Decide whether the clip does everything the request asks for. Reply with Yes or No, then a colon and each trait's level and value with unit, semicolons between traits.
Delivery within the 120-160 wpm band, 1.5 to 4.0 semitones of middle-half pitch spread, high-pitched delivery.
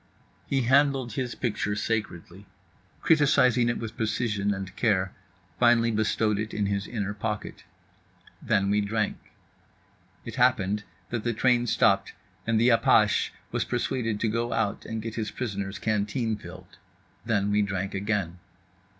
No: average, 140 wpm; average, 2.7 semitones; low, 110 Hz